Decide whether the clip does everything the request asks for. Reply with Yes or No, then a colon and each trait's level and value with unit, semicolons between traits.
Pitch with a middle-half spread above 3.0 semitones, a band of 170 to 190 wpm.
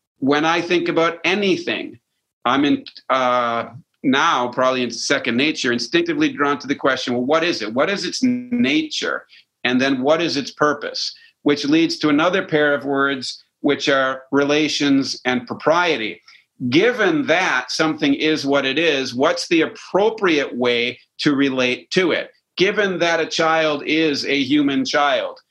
No: average, 4.3 semitones; average, 160 wpm